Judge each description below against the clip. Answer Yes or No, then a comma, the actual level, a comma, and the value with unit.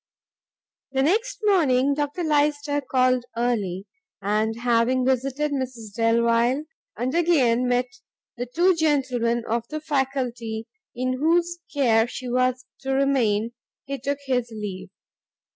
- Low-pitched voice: No, very high, 255 Hz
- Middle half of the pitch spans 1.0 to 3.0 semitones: No, average, 3.6 semitones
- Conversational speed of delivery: No, slow, 125 wpm